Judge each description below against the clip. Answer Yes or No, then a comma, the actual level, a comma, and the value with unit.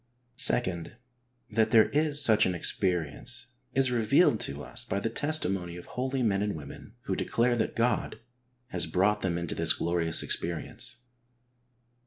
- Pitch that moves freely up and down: Yes, wide, 5.9 semitones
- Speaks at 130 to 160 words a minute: No, average, 170 wpm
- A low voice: Yes, low, 105 Hz